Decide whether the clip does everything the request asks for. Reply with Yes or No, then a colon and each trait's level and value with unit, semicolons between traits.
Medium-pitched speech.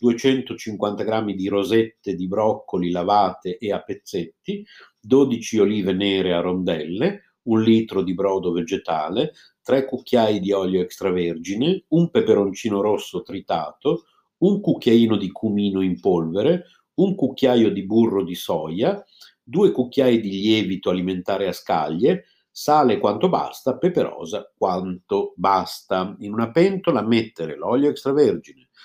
No: low, 105 Hz